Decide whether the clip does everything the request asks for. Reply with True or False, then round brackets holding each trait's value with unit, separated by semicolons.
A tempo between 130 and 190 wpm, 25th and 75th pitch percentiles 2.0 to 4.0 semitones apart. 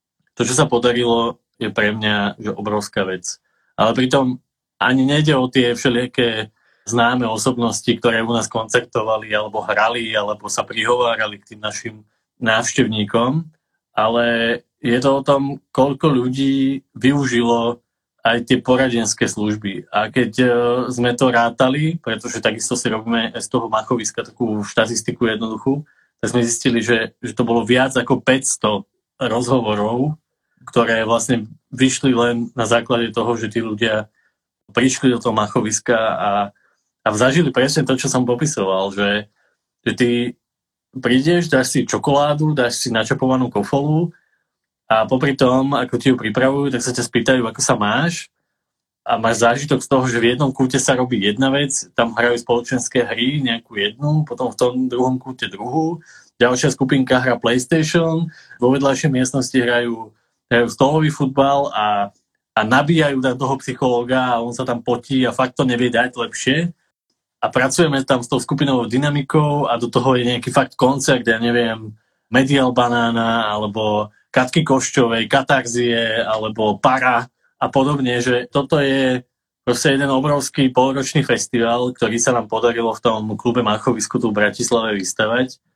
True (150 wpm; 2.5 semitones)